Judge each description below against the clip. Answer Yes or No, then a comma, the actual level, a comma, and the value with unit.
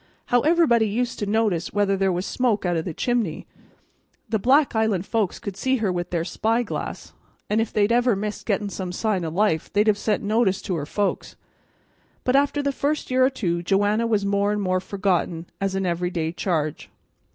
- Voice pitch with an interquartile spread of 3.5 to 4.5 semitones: Yes, average, 3.8 semitones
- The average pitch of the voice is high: Yes, high, 205 Hz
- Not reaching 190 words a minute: No, fast, 205 wpm